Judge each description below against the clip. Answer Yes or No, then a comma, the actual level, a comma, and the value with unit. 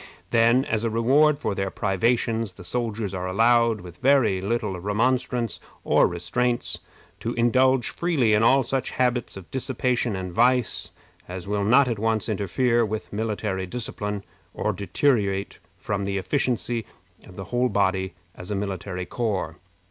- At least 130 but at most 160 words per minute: Yes, average, 150 wpm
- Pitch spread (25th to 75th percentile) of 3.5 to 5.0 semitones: Yes, average, 4.0 semitones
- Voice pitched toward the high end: No, low, 110 Hz